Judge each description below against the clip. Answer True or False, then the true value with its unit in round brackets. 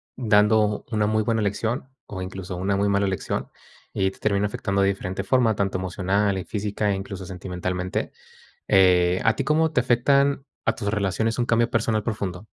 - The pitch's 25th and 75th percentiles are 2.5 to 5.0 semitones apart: True (2.8 semitones)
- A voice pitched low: True (100 Hz)